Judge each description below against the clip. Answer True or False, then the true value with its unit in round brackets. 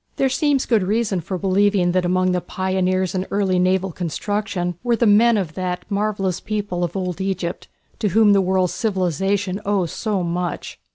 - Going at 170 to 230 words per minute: True (175 wpm)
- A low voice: False (190 Hz)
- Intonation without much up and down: True (2.2 semitones)